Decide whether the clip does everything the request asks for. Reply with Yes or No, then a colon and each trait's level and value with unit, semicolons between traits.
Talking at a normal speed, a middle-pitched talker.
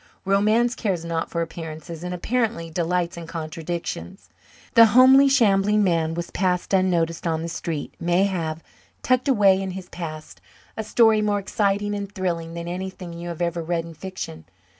Yes: average, 165 wpm; medium, 180 Hz